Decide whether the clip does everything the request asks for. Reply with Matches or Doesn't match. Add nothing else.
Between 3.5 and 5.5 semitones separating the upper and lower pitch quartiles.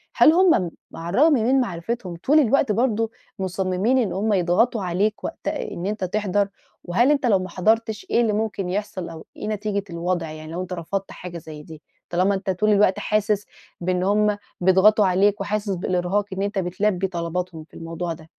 Doesn't match